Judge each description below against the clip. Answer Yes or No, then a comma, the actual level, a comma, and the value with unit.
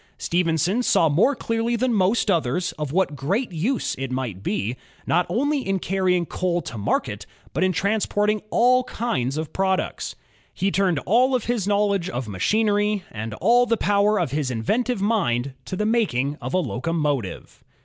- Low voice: No, medium, 185 Hz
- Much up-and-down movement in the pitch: Yes, wide, 7.1 semitones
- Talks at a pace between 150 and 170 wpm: Yes, average, 165 wpm